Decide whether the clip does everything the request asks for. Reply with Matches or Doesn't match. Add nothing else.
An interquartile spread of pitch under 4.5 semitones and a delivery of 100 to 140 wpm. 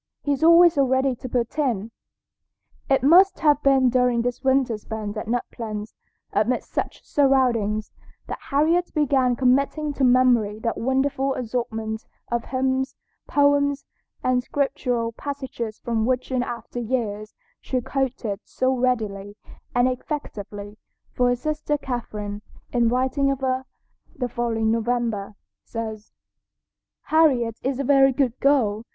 Matches